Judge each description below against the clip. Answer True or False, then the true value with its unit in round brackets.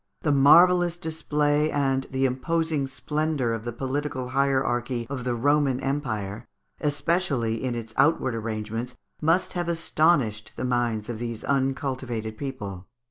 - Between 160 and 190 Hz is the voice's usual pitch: False (135 Hz)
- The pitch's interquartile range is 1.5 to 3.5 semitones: False (4.0 semitones)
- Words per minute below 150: True (135 wpm)